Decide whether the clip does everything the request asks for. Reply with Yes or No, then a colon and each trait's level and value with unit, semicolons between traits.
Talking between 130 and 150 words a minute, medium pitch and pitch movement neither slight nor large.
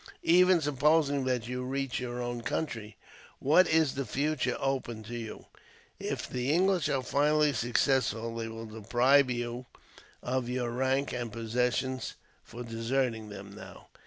No: average, 145 wpm; low, 125 Hz; average, 3.1 semitones